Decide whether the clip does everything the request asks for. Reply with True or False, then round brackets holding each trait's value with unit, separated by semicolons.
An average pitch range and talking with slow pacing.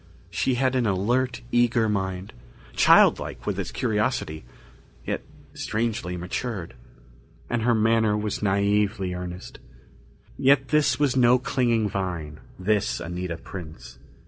True (4.9 semitones; 120 wpm)